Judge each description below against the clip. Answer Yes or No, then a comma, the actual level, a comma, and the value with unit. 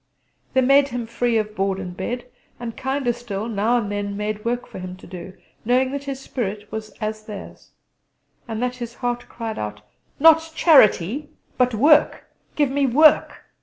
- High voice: Yes, high, 235 Hz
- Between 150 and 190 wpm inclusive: Yes, average, 170 wpm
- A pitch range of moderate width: Yes, average, 4.0 semitones